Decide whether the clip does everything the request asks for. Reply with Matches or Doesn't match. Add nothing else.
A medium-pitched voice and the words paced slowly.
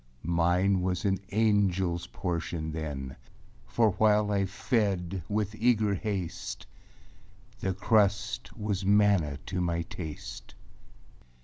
Doesn't match